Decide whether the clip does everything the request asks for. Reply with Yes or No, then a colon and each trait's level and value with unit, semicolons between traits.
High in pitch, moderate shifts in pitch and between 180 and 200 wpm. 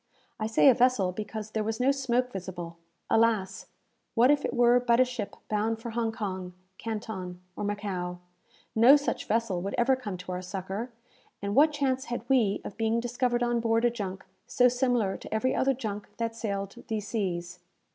Yes: high, 225 Hz; average, 3.6 semitones; average, 185 wpm